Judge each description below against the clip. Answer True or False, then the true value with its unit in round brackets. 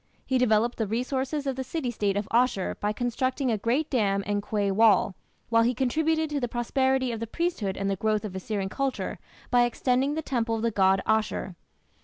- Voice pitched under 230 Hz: False (235 Hz)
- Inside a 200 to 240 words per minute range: True (205 wpm)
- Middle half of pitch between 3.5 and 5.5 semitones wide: True (4.0 semitones)